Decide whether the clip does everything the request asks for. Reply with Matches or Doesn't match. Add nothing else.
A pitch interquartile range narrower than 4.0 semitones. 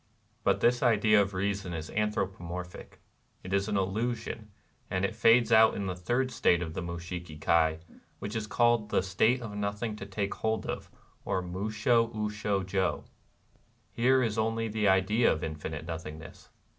Matches